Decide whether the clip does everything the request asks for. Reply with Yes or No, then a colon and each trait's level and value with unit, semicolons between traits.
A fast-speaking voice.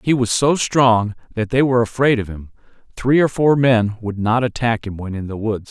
Yes: fast, 230 wpm